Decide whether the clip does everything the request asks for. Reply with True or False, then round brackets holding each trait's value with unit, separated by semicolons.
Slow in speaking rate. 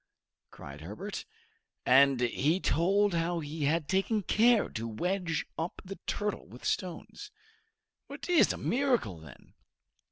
True (130 wpm)